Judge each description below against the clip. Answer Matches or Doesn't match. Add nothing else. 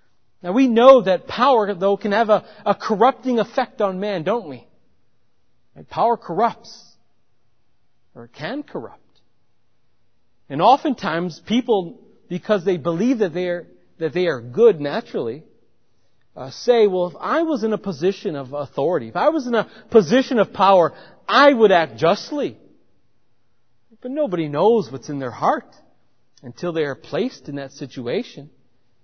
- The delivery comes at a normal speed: Matches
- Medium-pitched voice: Matches